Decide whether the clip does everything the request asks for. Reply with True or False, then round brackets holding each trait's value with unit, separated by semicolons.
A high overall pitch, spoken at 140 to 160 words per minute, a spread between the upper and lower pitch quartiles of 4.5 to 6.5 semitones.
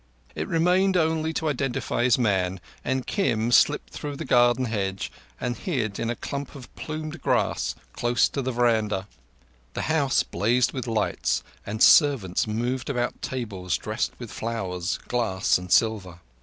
False (120 Hz; 155 wpm; 5.0 semitones)